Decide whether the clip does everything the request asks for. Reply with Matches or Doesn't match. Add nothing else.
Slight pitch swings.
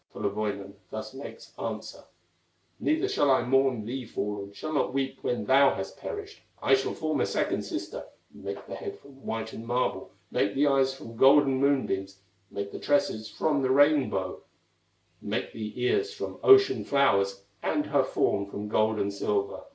Doesn't match